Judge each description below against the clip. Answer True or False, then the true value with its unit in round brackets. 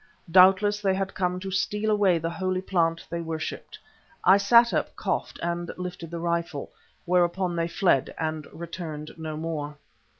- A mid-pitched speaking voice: True (175 Hz)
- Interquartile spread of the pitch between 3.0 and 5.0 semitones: False (2.5 semitones)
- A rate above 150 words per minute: True (160 wpm)